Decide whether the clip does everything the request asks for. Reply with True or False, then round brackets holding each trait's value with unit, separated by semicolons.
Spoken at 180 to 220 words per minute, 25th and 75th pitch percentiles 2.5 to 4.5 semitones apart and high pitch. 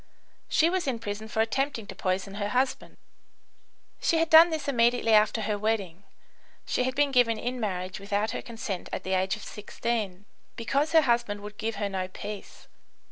True (185 wpm; 3.7 semitones; 220 Hz)